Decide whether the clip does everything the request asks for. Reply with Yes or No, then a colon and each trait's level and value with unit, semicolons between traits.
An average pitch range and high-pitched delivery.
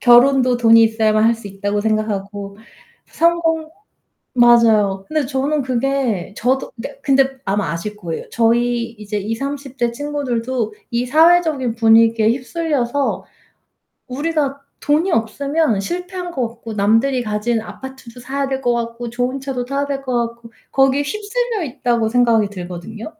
Yes: average, 3.7 semitones; high, 240 Hz